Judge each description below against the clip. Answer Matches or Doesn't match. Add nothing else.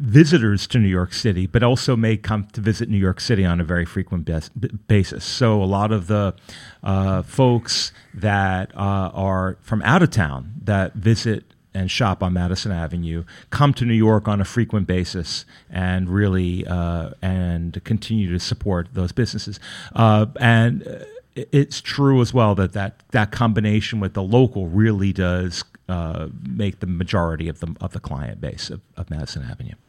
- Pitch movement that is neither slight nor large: Matches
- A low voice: Matches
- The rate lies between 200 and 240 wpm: Doesn't match